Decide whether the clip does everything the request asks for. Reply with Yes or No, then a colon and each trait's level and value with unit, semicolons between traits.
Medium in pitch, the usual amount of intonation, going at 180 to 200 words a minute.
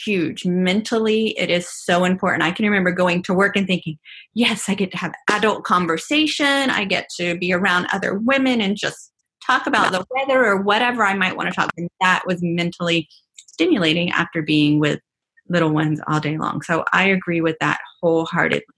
Yes: medium, 180 Hz; average, 3.3 semitones; average, 190 wpm